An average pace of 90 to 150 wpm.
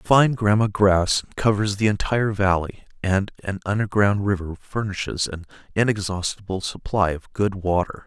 Yes: slow, 135 wpm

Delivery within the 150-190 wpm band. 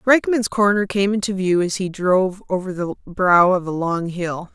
No: average, 200 wpm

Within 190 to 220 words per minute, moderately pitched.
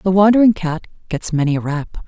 Yes: fast, 205 wpm; medium, 175 Hz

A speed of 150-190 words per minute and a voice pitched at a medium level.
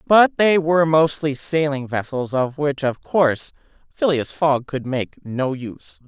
Yes: average, 160 wpm; medium, 145 Hz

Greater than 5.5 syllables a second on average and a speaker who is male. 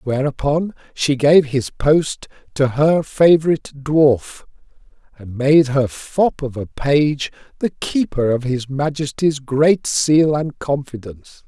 No: 3.6 syllables/s; male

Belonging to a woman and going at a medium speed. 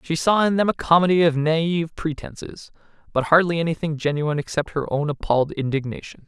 No: male; average, 170 wpm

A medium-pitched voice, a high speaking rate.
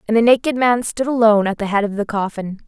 No: high, 220 Hz; fast, 270 wpm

